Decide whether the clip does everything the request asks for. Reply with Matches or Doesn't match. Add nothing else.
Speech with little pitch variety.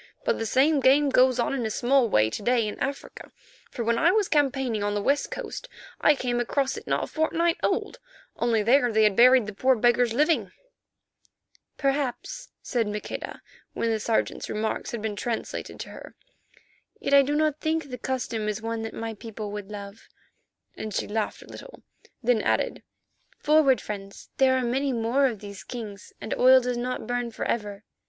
Doesn't match